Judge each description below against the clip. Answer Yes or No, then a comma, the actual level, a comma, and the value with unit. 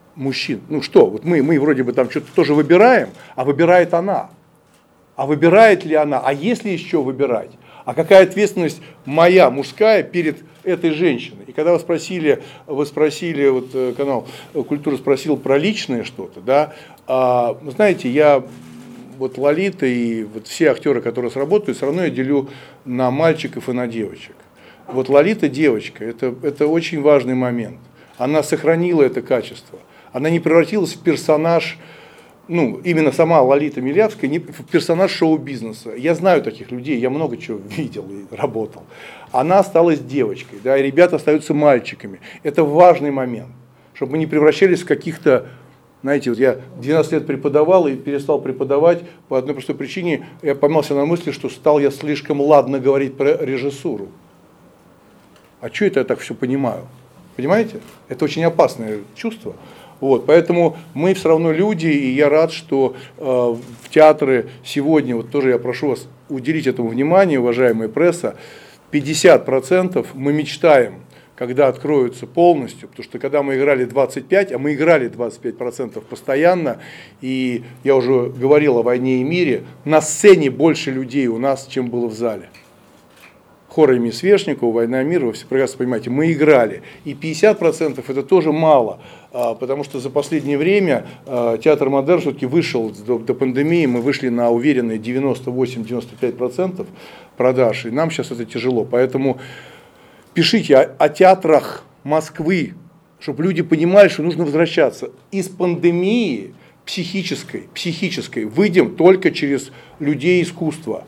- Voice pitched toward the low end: No, medium, 145 Hz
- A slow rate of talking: No, average, 145 wpm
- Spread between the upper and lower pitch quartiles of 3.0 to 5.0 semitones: Yes, average, 4.3 semitones